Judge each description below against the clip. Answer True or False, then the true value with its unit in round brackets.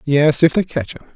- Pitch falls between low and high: True (150 Hz)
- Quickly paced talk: True (210 wpm)